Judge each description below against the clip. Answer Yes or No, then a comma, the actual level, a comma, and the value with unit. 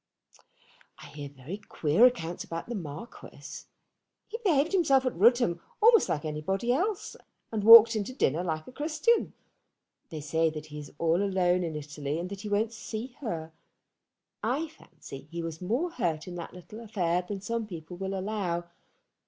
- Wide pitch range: Yes, wide, 6.4 semitones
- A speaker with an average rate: Yes, average, 170 wpm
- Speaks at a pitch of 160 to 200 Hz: Yes, high, 190 Hz